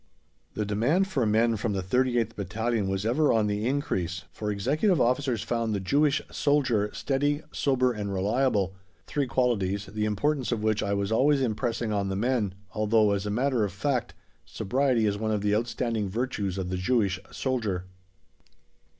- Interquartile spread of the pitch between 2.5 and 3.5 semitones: No, average, 4.1 semitones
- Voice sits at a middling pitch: No, low, 110 Hz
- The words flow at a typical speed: Yes, average, 170 wpm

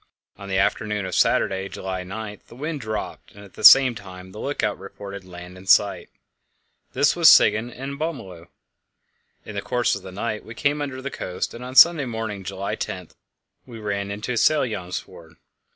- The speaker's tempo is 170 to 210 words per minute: Yes, average, 180 wpm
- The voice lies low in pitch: Yes, low, 105 Hz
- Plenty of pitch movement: No, average, 4.4 semitones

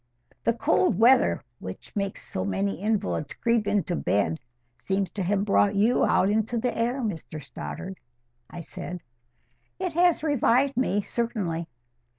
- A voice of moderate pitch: No, high, 205 Hz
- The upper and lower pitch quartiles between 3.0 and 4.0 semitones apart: No, average, 5.0 semitones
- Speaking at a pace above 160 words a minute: No, average, 145 wpm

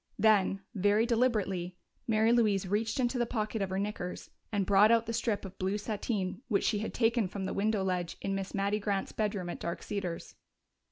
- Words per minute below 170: No, average, 200 wpm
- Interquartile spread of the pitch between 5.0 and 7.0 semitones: No, narrow, 2.4 semitones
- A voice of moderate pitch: No, high, 205 Hz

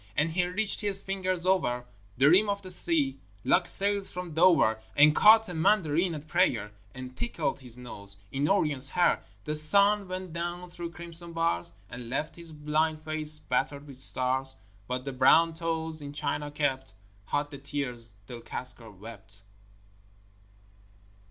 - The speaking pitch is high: No, medium, 155 Hz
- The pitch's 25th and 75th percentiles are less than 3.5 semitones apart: No, average, 5.3 semitones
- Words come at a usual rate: Yes, average, 160 wpm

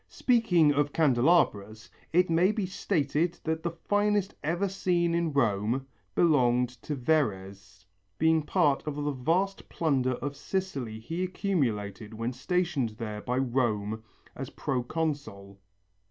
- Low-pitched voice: No, medium, 145 Hz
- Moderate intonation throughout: No, wide, 6.4 semitones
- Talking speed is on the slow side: Yes, slow, 125 wpm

